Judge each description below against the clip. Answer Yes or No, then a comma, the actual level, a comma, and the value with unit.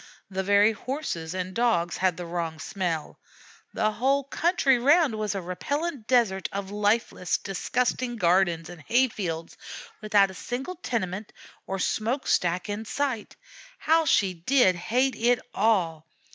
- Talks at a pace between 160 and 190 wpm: No, average, 145 wpm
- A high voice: Yes, high, 205 Hz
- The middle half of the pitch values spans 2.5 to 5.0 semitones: No, wide, 5.5 semitones